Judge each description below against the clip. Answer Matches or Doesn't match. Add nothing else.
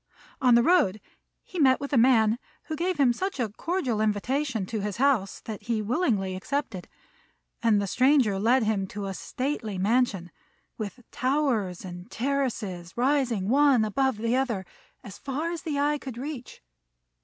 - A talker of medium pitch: Doesn't match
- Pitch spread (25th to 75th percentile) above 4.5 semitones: Matches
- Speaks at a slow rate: Doesn't match